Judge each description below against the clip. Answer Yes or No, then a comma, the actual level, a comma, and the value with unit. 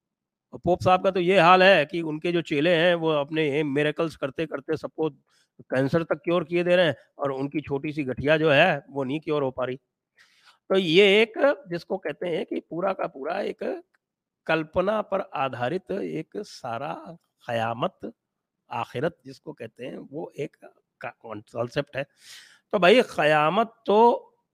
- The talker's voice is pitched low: No, medium, 155 Hz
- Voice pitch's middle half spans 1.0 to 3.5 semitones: No, average, 4.4 semitones